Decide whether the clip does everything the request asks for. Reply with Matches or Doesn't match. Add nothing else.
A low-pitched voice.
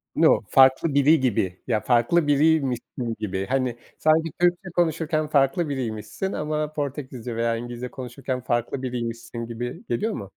Matches